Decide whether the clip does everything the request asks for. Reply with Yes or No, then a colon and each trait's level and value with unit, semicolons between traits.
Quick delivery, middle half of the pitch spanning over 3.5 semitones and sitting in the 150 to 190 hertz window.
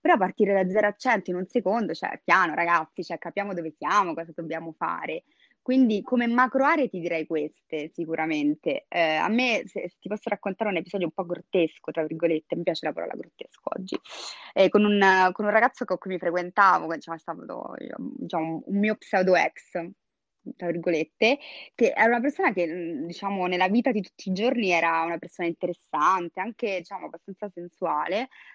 Yes: fast, 185 wpm; average, 4.4 semitones; medium, 185 Hz